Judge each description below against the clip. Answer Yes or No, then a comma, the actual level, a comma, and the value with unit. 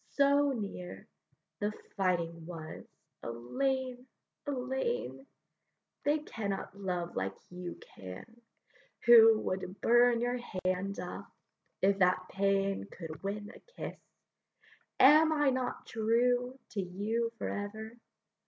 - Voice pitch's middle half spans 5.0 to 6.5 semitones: Yes, wide, 5.4 semitones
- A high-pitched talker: Yes, high, 210 Hz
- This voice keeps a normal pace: No, slow, 110 wpm